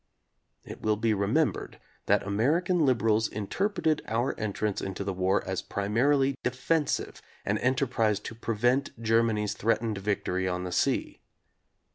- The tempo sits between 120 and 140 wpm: Yes, slow, 135 wpm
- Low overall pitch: Yes, low, 110 Hz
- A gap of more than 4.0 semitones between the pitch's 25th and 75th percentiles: Yes, average, 4.5 semitones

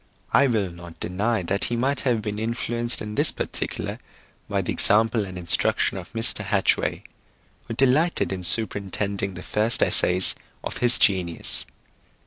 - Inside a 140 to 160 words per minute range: Yes, average, 150 wpm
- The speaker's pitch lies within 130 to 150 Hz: No, low, 105 Hz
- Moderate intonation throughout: Yes, average, 3.8 semitones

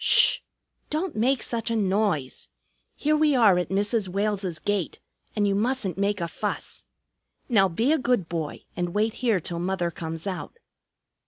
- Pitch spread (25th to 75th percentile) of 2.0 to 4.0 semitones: No, average, 4.5 semitones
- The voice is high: Yes, high, 200 Hz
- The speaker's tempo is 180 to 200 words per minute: No, average, 165 wpm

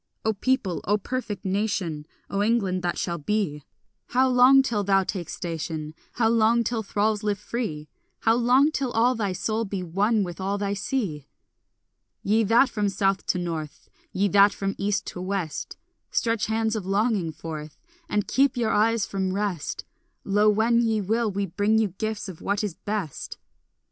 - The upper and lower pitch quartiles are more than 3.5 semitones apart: No, average, 3.2 semitones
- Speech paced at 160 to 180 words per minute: Yes, average, 175 wpm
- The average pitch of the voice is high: Yes, high, 205 Hz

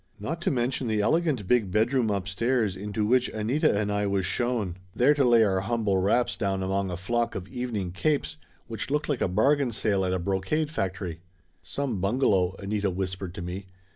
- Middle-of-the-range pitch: No, low, 105 Hz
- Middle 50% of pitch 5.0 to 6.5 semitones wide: No, average, 4.4 semitones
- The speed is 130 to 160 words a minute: No, average, 190 wpm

